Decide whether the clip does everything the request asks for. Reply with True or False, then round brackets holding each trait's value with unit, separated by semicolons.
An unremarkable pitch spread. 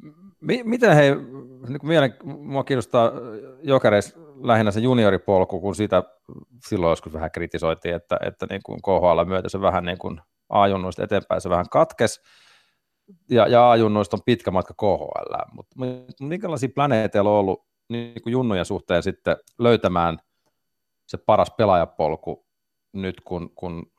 False (6.1 semitones)